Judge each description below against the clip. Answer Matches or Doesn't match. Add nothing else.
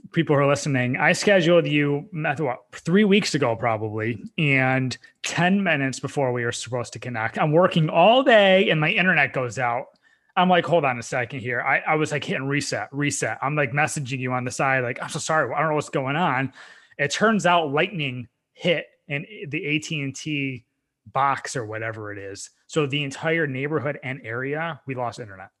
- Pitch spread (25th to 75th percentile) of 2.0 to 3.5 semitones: Doesn't match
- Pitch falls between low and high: Matches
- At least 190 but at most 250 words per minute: Matches